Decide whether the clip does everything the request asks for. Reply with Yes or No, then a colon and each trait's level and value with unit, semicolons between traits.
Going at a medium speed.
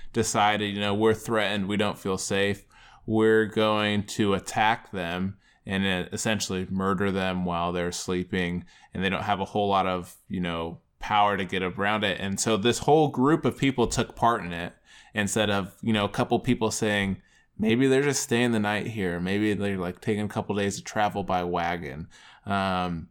Yes: average, 190 wpm